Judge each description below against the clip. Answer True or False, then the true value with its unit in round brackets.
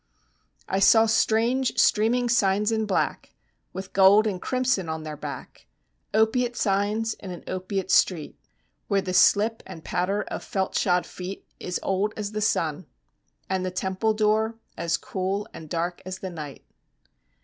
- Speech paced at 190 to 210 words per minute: False (155 wpm)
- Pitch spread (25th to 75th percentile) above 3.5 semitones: False (3.0 semitones)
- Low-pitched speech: False (195 Hz)